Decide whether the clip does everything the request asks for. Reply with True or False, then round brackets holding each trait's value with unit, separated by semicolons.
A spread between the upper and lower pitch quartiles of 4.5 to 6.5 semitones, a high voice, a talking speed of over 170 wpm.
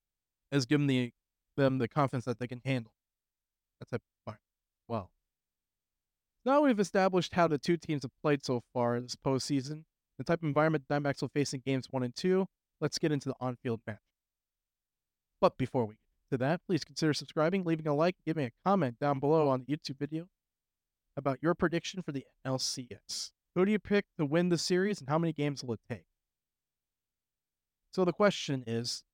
False (4.9 semitones; 145 Hz; 200 wpm)